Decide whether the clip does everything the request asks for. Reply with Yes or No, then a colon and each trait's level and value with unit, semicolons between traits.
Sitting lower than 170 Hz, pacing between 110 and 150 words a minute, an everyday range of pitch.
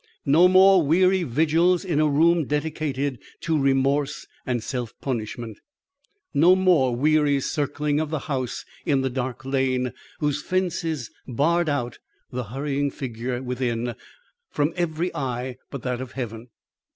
Yes: medium, 140 Hz; average, 140 wpm; average, 4.0 semitones